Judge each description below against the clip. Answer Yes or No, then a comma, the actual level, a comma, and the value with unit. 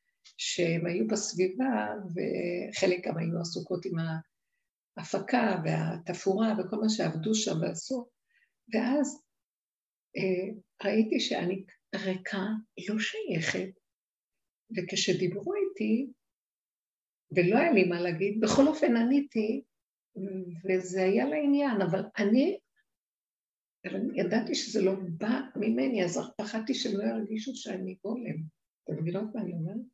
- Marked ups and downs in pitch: No, average, 4.1 semitones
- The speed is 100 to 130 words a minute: Yes, average, 110 wpm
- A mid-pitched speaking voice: No, high, 205 Hz